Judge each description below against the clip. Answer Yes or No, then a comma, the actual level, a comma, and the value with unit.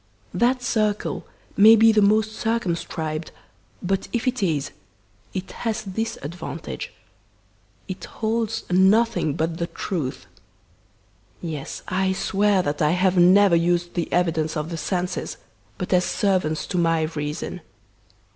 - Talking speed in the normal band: No, slow, 130 wpm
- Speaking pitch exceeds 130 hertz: Yes, medium, 185 Hz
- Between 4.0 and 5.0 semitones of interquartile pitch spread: Yes, average, 4.4 semitones